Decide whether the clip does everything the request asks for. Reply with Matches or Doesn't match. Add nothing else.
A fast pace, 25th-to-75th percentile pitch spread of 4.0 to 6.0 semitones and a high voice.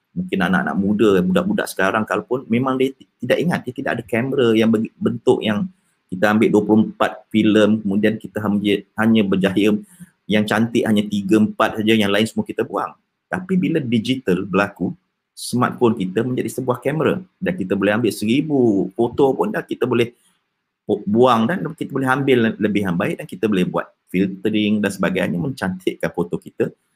Doesn't match